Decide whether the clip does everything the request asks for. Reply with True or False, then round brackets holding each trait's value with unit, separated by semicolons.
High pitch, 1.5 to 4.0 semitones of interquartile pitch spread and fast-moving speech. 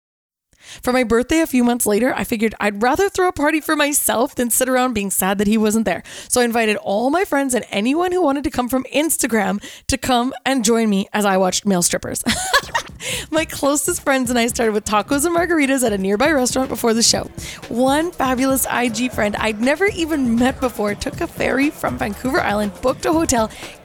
False (250 Hz; 4.6 semitones; 210 wpm)